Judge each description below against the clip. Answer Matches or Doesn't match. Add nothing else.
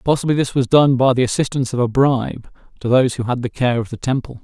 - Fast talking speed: Matches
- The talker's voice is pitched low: Matches